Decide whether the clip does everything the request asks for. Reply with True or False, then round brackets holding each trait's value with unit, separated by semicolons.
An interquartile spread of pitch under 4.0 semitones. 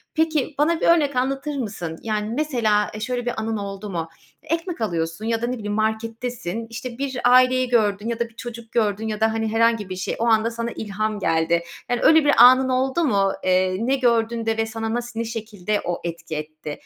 True (3.2 semitones)